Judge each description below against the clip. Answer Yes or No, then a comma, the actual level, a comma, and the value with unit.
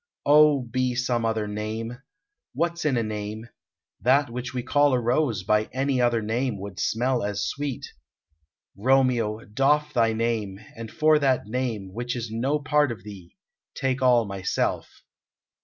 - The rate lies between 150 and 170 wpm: Yes, average, 155 wpm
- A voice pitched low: Yes, low, 120 Hz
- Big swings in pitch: No, average, 3.7 semitones